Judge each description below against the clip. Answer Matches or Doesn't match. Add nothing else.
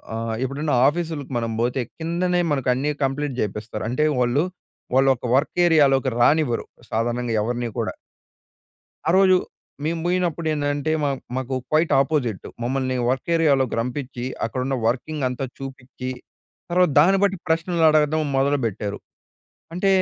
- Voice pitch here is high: Doesn't match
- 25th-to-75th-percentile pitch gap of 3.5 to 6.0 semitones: Matches